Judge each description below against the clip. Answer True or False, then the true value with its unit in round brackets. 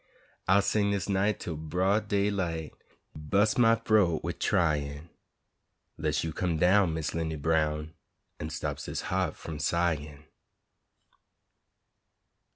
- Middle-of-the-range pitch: False (85 Hz)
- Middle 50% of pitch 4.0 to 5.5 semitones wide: True (4.4 semitones)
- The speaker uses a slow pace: True (130 wpm)